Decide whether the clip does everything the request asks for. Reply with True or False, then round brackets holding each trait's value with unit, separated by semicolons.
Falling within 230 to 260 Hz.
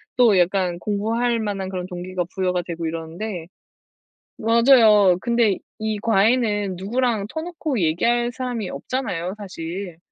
False (205 Hz)